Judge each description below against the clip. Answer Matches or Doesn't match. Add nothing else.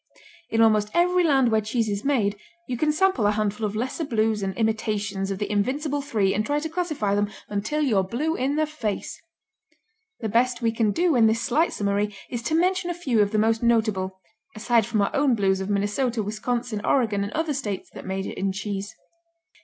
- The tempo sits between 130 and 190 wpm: Doesn't match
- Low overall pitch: Doesn't match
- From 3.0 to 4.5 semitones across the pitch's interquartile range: Doesn't match